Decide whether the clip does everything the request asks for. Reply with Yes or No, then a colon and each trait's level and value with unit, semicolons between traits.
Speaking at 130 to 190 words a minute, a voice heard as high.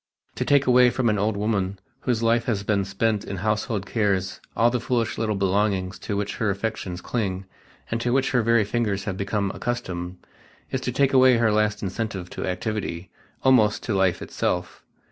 No: average, 185 wpm; low, 105 Hz